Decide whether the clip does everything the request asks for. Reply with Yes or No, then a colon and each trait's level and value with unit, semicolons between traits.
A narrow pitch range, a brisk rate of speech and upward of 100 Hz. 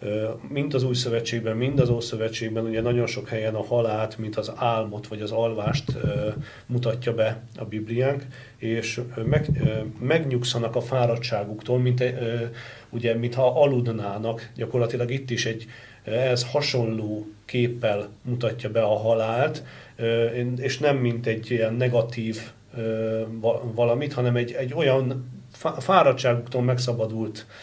No: narrow, 2.1 semitones; average, 125 wpm; low, 120 Hz